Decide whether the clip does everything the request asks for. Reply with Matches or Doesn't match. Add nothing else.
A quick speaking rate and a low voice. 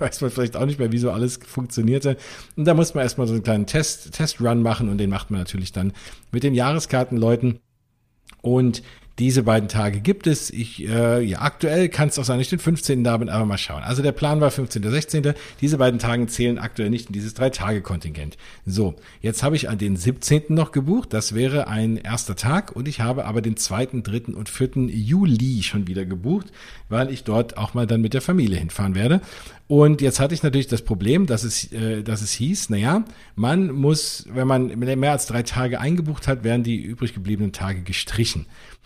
Matches